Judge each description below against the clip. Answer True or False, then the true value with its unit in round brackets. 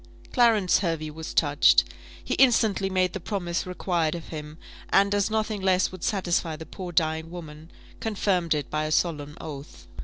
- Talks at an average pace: True (165 wpm)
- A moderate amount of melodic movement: True (3.6 semitones)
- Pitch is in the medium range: True (175 Hz)